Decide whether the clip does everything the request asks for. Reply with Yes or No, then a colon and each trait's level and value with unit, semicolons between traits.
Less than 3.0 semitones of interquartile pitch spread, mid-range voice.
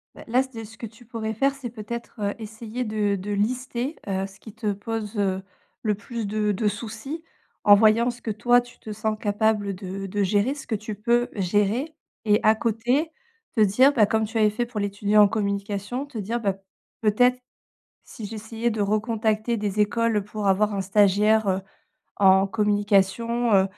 No: narrow, 2.4 semitones; high, 215 Hz